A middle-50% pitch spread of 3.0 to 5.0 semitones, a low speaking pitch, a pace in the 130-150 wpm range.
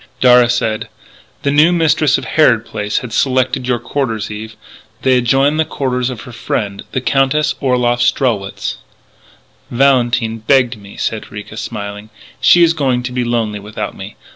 No: average, 3.4 semitones; low, 125 Hz; average, 160 wpm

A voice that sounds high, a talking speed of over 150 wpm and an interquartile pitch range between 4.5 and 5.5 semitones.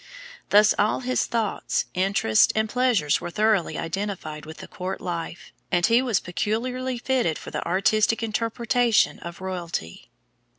No: high, 205 Hz; average, 140 wpm; average, 4.9 semitones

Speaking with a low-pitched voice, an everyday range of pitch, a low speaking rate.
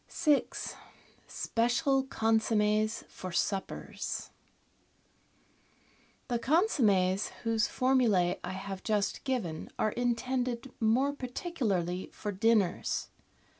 No: high, 225 Hz; average, 4.3 semitones; slow, 90 wpm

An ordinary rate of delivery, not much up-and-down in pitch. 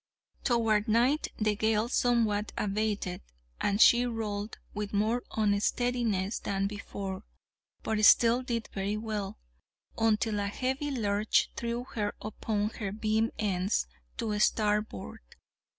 No: slow, 120 wpm; narrow, 2.1 semitones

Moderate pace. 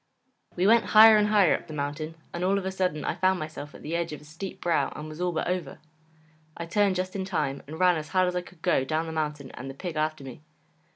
No: fast, 270 wpm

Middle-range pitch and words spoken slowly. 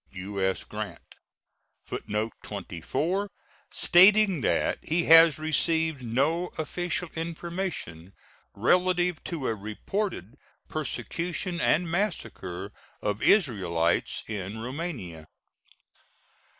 Yes: medium, 155 Hz; slow, 85 wpm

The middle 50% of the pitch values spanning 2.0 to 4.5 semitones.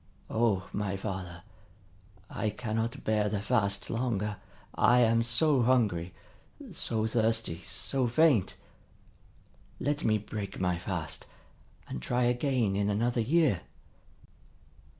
Yes: average, 3.6 semitones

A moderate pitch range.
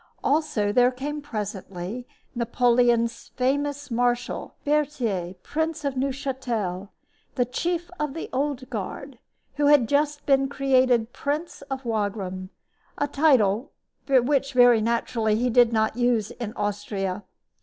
Yes: average, 4.4 semitones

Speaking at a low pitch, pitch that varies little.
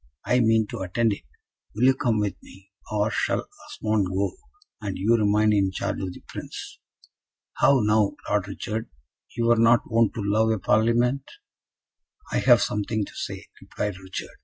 Yes: low, 110 Hz; narrow, 2.3 semitones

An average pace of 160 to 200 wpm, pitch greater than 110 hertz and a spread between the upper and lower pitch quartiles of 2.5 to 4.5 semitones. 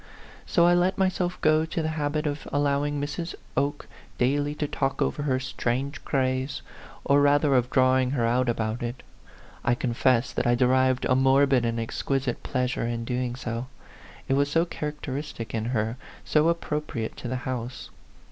Yes: average, 165 wpm; low, 135 Hz; average, 2.9 semitones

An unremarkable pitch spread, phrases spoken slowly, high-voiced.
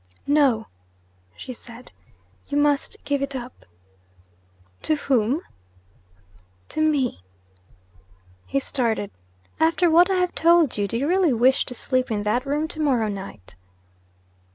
Yes: average, 4.8 semitones; slow, 130 wpm; very high, 275 Hz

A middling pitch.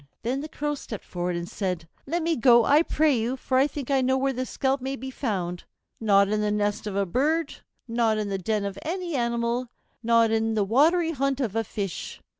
No: high, 235 Hz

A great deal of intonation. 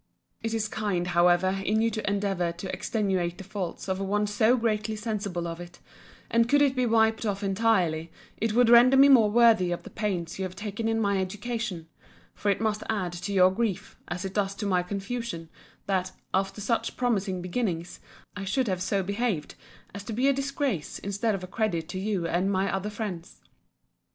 No: average, 3.3 semitones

